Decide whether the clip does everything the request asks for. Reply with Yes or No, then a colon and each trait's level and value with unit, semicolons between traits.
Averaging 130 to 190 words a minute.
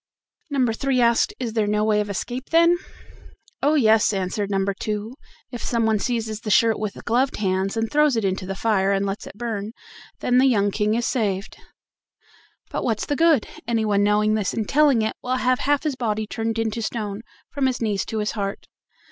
No: average, 200 wpm